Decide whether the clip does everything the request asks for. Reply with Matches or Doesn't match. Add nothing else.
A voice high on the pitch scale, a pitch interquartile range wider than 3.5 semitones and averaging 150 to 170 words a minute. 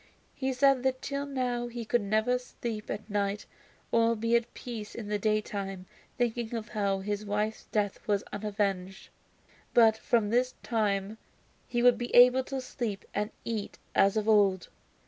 Doesn't match